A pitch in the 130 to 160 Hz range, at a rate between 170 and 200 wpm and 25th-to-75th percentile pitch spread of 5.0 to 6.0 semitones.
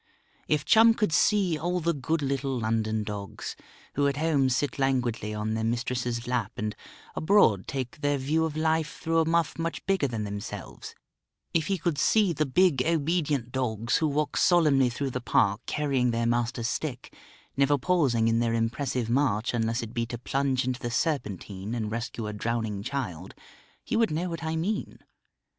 Yes: low, 135 Hz; average, 180 wpm; wide, 5.4 semitones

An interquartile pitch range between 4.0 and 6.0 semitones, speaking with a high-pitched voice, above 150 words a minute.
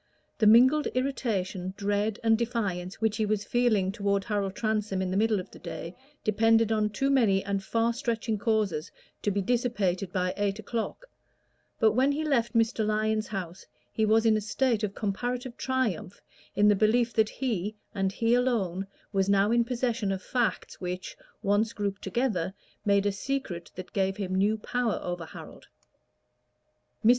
No: average, 3.2 semitones; high, 215 Hz; average, 170 wpm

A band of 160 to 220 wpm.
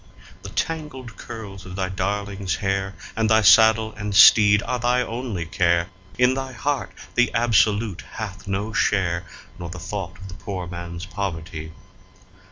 No: average, 150 wpm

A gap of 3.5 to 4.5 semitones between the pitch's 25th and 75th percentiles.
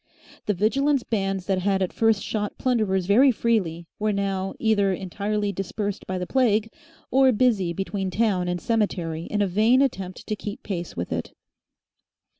No: average, 2.9 semitones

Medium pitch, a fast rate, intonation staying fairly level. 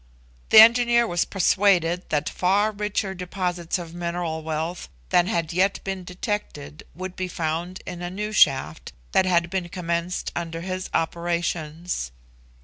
No: medium, 175 Hz; average, 140 wpm; narrow, 2.2 semitones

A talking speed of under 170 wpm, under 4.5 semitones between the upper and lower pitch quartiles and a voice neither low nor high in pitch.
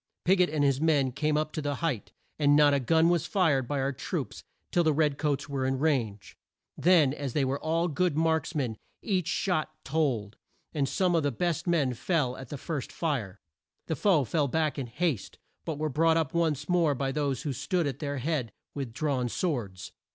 No: fast, 205 wpm; average, 3.4 semitones; medium, 145 Hz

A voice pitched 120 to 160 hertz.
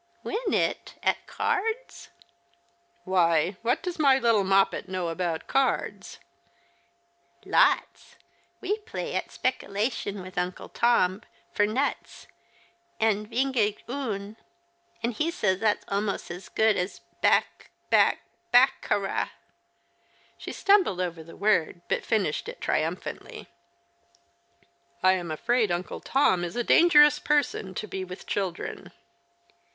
No: high, 210 Hz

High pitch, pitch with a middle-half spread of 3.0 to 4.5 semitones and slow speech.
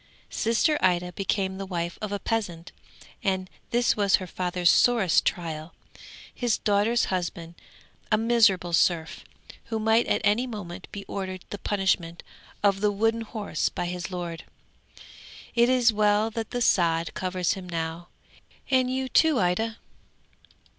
No: high, 195 Hz; average, 4.1 semitones; average, 145 wpm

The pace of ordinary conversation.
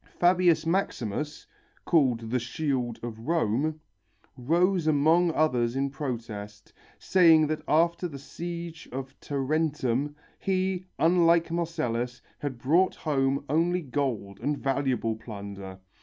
No: slow, 110 wpm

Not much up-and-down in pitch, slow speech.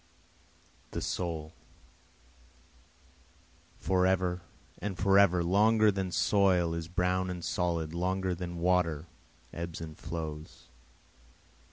Yes: narrow, 1.9 semitones; slow, 95 wpm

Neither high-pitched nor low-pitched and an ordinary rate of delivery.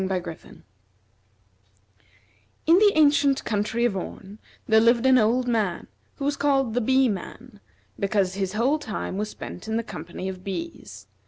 No: high, 220 Hz; average, 150 wpm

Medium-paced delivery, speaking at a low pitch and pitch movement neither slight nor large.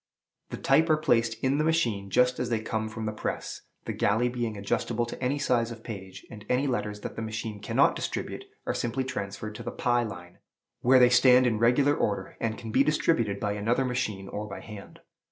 No: fast, 210 wpm; low, 115 Hz; average, 3.0 semitones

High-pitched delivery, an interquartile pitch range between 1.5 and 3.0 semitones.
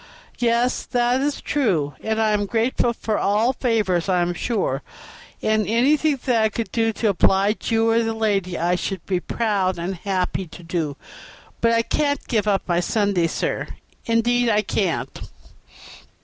No: high, 215 Hz; average, 3.9 semitones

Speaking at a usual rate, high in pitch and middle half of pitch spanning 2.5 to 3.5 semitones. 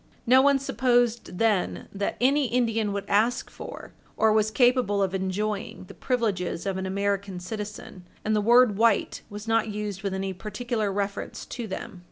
Yes: average, 170 wpm; high, 210 Hz; average, 3.1 semitones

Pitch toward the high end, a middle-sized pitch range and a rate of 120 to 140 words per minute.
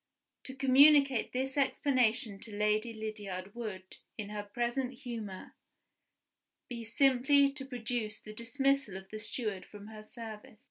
Yes: high, 230 Hz; average, 3.9 semitones; slow, 135 wpm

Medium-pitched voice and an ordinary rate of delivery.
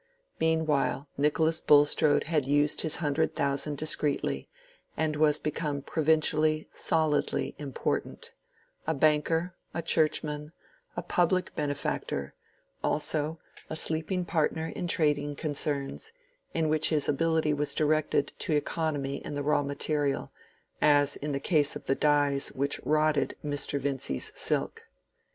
No: medium, 150 Hz; slow, 125 wpm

